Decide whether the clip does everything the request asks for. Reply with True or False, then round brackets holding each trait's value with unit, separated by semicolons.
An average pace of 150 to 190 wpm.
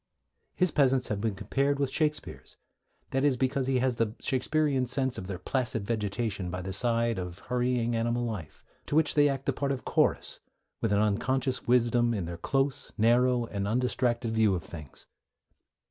True (175 wpm)